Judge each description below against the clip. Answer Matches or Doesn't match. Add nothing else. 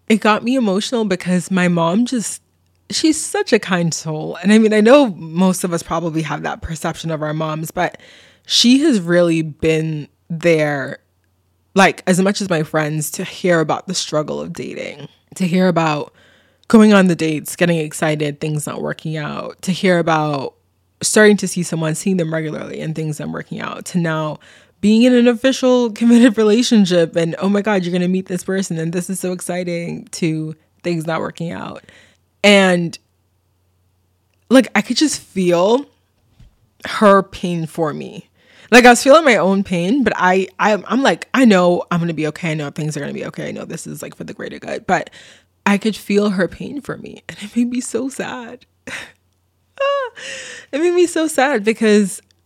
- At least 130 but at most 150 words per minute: Doesn't match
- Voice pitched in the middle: Matches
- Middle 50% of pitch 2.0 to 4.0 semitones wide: Doesn't match